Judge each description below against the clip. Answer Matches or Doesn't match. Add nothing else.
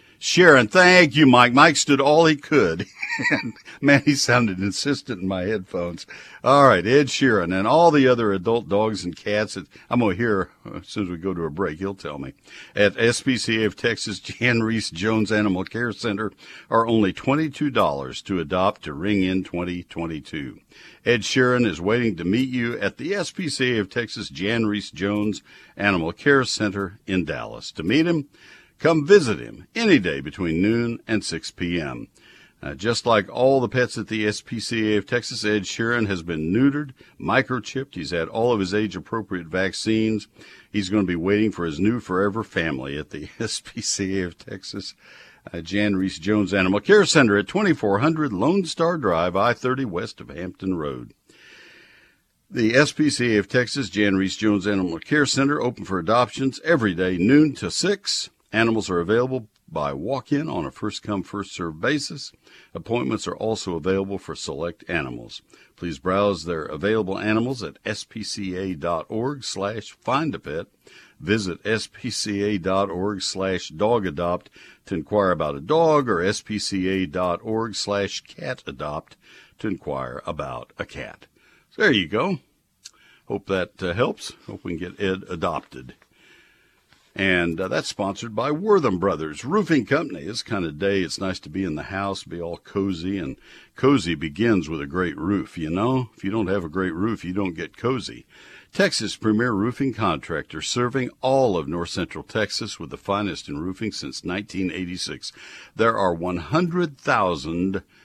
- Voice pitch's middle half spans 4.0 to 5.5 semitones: Matches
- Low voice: Matches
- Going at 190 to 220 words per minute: Doesn't match